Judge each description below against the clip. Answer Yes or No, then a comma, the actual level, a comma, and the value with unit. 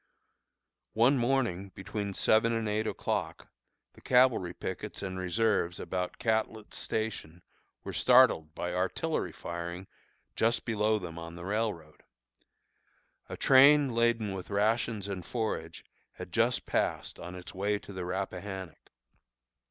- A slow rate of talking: Yes, slow, 130 wpm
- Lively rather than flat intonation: No, average, 4.0 semitones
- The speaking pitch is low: Yes, low, 100 Hz